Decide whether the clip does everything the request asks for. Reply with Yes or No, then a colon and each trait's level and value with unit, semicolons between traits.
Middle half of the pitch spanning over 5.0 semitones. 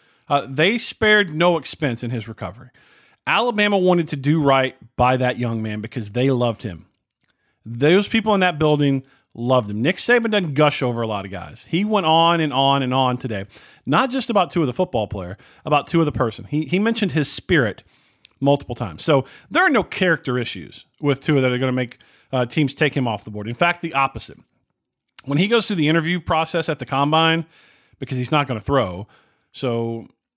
Yes: wide, 5.5 semitones